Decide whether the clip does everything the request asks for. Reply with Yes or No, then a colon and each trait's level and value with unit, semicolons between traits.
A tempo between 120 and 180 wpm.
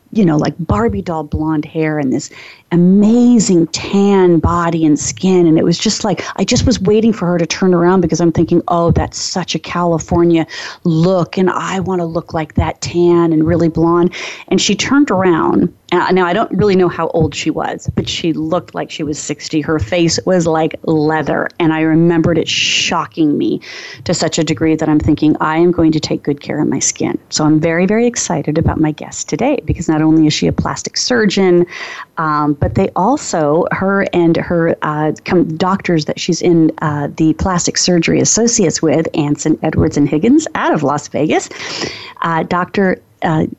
No: average, 195 wpm